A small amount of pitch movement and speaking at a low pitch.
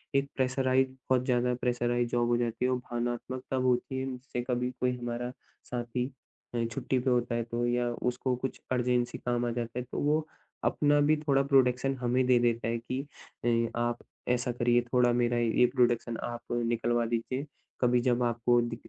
Yes: narrow, 1.1 semitones; low, 120 Hz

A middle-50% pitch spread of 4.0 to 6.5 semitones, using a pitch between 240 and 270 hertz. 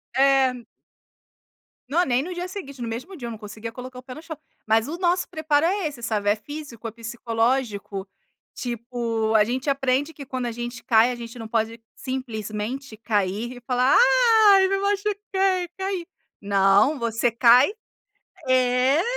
Yes: average, 4.3 semitones; very high, 250 Hz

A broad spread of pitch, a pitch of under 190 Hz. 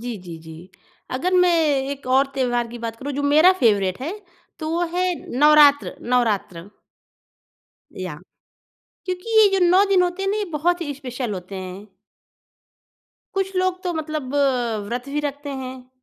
No: wide, 6.9 semitones; very high, 280 Hz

